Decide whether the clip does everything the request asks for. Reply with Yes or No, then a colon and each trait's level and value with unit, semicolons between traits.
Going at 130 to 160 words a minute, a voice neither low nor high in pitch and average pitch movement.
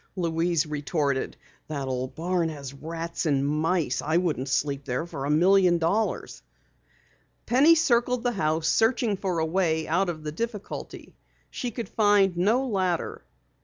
Yes: average, 150 wpm; medium, 170 Hz; average, 4.6 semitones